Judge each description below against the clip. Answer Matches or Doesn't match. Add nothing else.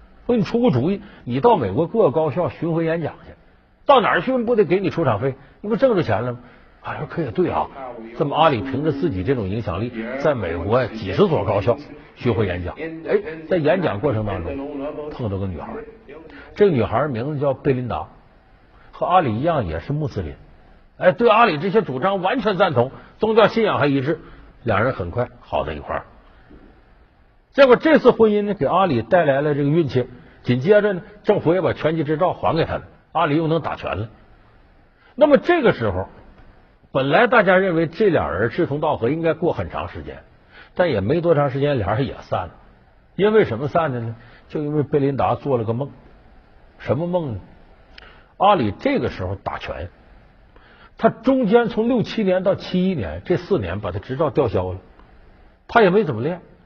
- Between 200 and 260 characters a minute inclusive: Doesn't match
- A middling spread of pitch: Doesn't match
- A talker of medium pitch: Matches